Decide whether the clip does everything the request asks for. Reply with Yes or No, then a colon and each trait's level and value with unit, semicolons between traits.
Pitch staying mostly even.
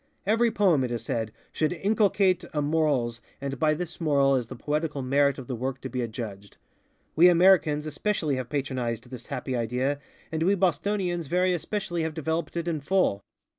No: average, 5.2 semitones